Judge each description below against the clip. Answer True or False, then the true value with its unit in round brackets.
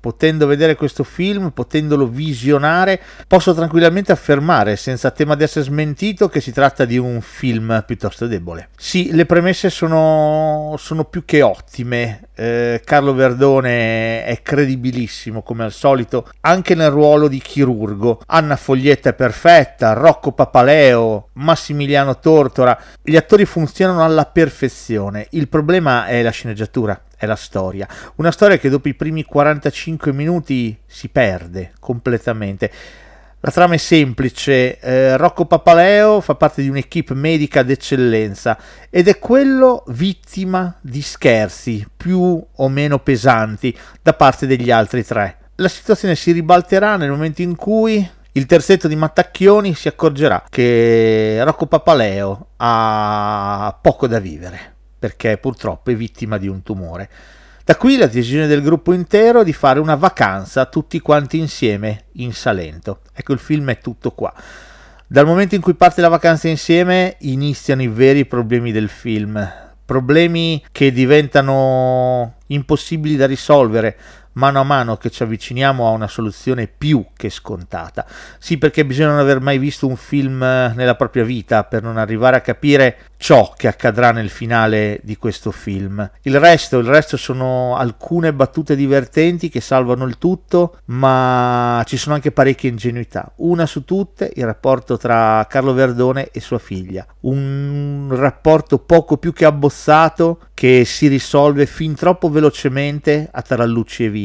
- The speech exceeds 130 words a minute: True (145 wpm)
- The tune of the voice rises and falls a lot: False (5.0 semitones)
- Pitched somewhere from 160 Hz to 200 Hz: False (135 Hz)